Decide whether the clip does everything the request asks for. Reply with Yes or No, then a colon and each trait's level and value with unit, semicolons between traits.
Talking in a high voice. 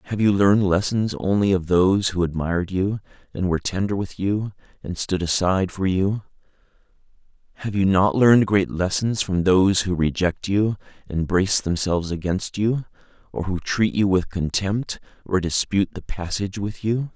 No: very low, 95 Hz